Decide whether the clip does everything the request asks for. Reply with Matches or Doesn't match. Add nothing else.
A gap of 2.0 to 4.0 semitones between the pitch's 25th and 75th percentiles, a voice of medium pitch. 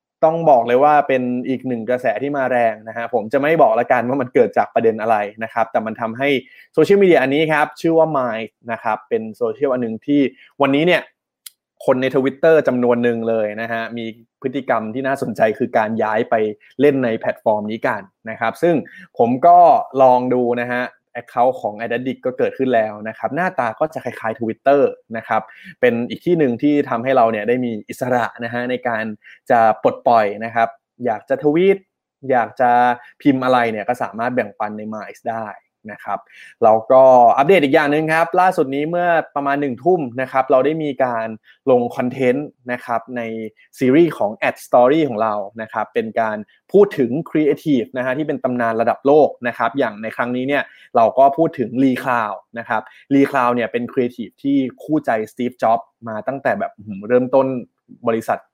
Doesn't match